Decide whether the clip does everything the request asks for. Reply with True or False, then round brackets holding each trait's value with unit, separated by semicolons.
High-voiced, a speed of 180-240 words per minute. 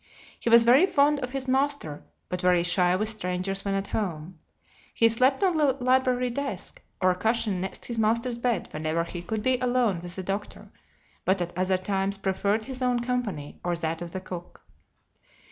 True (205 Hz; 190 wpm)